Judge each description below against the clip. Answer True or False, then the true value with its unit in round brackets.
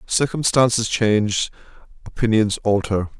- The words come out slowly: True (75 wpm)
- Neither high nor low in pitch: False (110 Hz)